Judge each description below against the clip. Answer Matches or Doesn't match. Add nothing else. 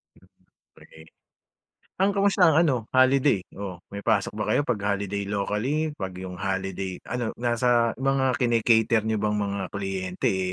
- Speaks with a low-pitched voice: Matches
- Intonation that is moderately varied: Matches